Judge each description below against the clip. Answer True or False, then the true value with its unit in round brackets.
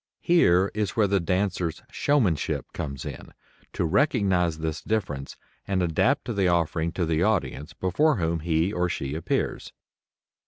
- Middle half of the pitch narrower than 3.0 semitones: False (3.8 semitones)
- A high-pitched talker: False (90 Hz)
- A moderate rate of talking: True (145 wpm)